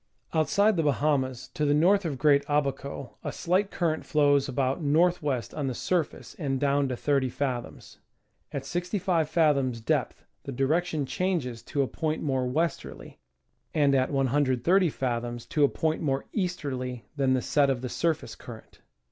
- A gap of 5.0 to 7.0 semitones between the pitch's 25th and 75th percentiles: No, average, 3.5 semitones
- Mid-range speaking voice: Yes, medium, 145 Hz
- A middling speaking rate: Yes, average, 170 wpm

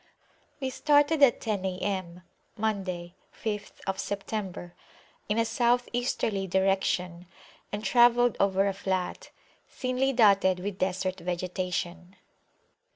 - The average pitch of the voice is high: Yes, high, 195 Hz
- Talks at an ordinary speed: No, slow, 105 wpm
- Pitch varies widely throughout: No, average, 3.8 semitones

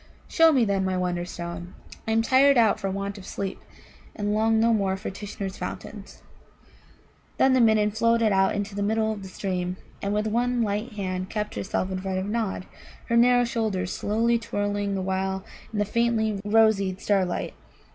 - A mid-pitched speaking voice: No, high, 205 Hz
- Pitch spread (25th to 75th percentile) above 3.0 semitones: No, average, 2.7 semitones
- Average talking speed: Yes, average, 180 wpm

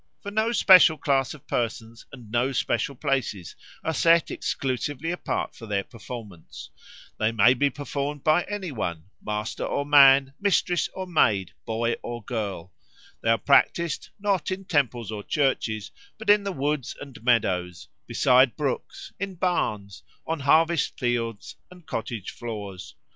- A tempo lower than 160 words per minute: Yes, average, 150 wpm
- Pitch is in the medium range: No, low, 130 Hz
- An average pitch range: No, wide, 6.1 semitones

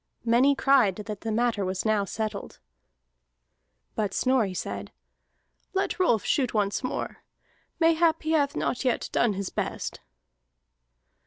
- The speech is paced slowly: Yes, slow, 130 wpm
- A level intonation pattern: No, average, 5.0 semitones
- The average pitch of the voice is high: Yes, high, 230 Hz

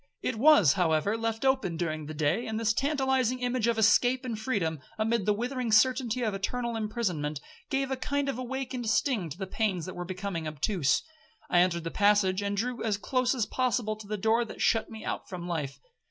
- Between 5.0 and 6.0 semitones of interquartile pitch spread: Yes, average, 5.3 semitones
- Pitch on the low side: No, high, 220 Hz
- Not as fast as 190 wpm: No, fast, 205 wpm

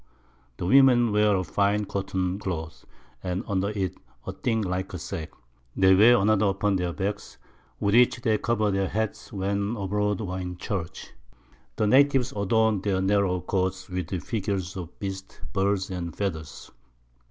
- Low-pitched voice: Yes, low, 100 Hz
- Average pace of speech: Yes, average, 160 wpm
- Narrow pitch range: Yes, narrow, 2.1 semitones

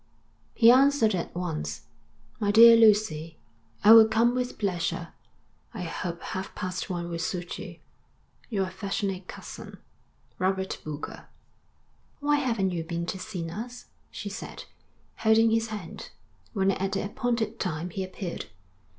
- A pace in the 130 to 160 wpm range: Yes, average, 140 wpm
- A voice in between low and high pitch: No, high, 195 Hz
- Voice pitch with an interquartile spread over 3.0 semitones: Yes, average, 4.1 semitones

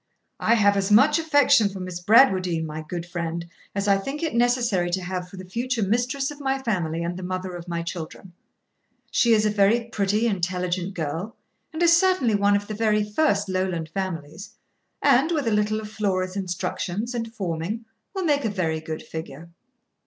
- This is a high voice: Yes, high, 200 Hz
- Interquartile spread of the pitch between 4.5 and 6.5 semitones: Yes, average, 4.8 semitones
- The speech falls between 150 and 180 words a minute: No, average, 190 wpm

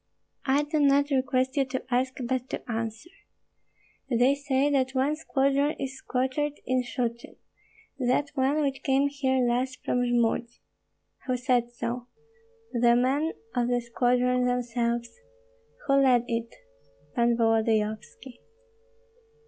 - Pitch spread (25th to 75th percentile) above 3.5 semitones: No, narrow, 2.4 semitones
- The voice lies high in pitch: Yes, very high, 255 Hz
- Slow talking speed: Yes, slow, 125 wpm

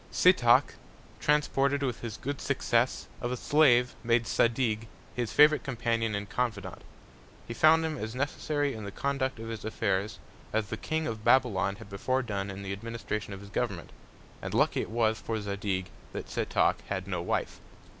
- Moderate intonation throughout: Yes, average, 4.3 semitones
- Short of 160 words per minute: No, average, 175 wpm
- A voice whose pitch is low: Yes, low, 115 Hz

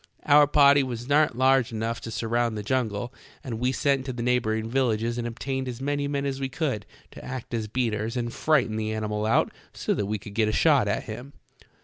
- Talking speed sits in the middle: No, fast, 220 wpm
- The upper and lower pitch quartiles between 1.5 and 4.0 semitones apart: Yes, average, 3.5 semitones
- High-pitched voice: No, low, 120 Hz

